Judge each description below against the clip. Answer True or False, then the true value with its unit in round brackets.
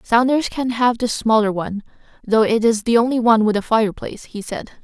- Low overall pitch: False (225 Hz)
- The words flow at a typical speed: False (210 wpm)